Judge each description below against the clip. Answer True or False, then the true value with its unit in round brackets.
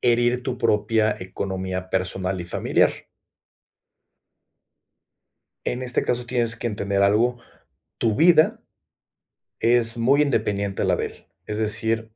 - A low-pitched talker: True (115 Hz)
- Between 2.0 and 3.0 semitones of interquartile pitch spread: False (3.5 semitones)